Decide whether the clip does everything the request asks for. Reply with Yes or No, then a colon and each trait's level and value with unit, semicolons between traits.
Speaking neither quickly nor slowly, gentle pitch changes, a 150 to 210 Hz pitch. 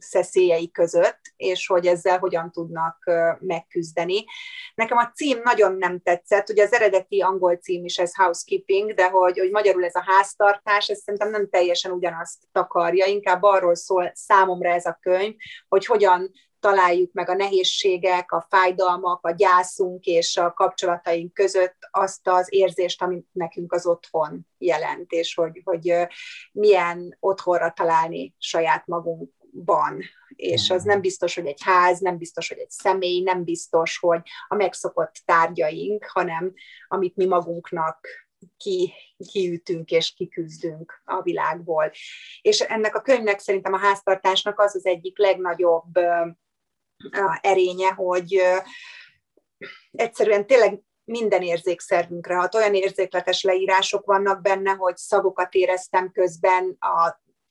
Yes: average, 135 wpm; narrow, 2.1 semitones; medium, 185 Hz